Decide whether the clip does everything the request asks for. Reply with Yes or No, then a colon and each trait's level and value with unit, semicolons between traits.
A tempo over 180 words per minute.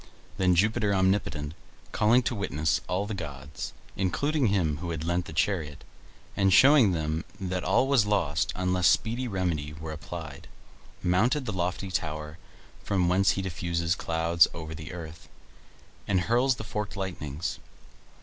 No: average, 150 wpm